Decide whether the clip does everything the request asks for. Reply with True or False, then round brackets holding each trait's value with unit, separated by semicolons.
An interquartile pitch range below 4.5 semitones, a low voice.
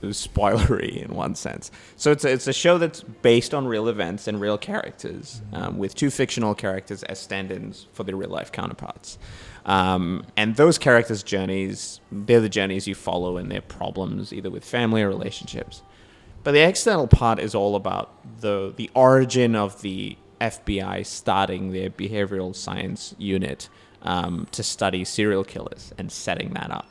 True (3.5 semitones; 105 Hz)